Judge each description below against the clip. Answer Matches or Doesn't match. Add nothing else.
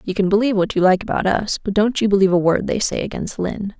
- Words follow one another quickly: Matches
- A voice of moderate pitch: Doesn't match